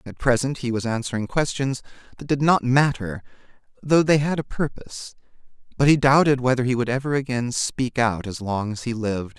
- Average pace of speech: Yes, average, 190 wpm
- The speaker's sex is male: Yes, male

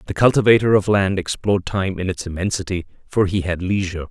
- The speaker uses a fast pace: No, average, 190 wpm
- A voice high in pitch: No, very low, 95 Hz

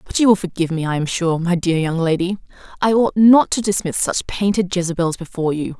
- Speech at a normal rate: No, fast, 230 wpm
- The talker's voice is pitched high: No, medium, 180 Hz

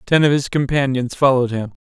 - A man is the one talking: Yes, male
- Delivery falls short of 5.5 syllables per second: No, 6.1 syllables/s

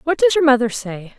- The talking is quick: Yes, fast, 255 wpm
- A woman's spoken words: Yes, female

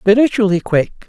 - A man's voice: Yes, male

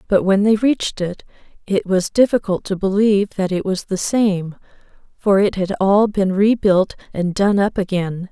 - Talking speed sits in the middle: Yes, average, 180 wpm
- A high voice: Yes, high, 195 Hz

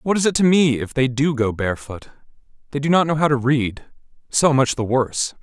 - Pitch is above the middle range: No, medium, 140 Hz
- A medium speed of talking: No, fast, 230 wpm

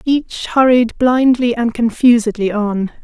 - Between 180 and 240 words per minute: No, slow, 120 wpm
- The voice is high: Yes, high, 235 Hz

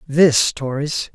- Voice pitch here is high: No, medium, 145 Hz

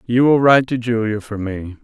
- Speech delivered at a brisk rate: Yes, fast, 230 wpm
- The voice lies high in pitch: No, low, 115 Hz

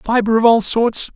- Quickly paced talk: Yes, fast, 210 wpm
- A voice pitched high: Yes, high, 225 Hz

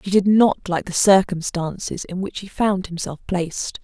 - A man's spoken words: No, female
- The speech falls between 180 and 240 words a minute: Yes, fast, 205 wpm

